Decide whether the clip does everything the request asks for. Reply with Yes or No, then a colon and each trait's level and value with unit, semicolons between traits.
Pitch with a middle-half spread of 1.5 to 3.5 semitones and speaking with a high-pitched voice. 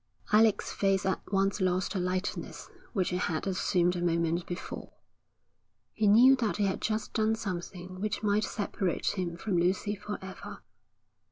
Yes: average, 2.7 semitones; high, 195 Hz